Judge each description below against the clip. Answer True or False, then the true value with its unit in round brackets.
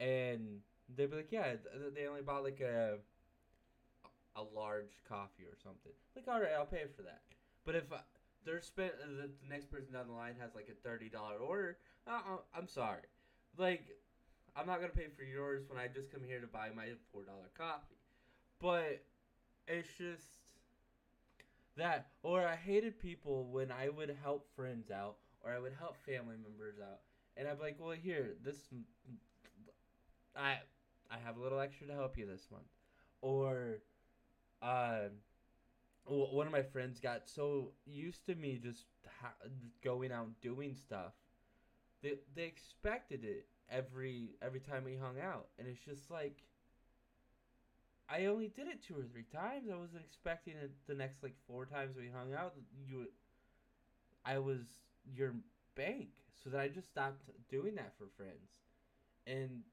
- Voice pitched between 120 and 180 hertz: True (135 Hz)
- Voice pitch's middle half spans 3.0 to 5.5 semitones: True (3.8 semitones)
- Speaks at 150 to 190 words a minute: True (165 wpm)